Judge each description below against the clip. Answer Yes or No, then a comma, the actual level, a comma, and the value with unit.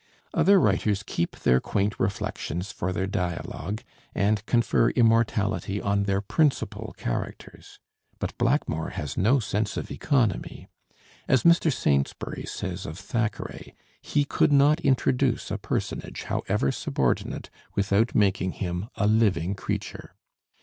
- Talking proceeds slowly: Yes, slow, 125 wpm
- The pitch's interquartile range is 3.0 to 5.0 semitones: Yes, average, 4.1 semitones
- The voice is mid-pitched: No, low, 100 Hz